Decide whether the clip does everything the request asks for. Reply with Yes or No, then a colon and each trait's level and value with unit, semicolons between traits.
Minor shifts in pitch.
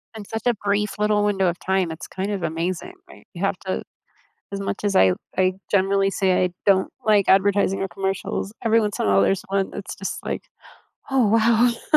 Yes: narrow, 1.7 semitones